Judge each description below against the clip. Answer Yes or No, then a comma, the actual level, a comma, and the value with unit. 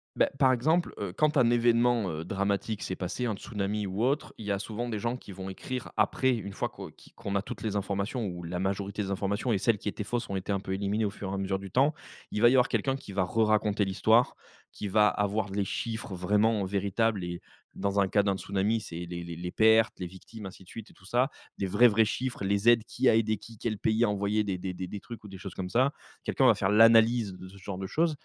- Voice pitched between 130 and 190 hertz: No, low, 105 Hz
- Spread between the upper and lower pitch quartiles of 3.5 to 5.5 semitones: No, average, 2.9 semitones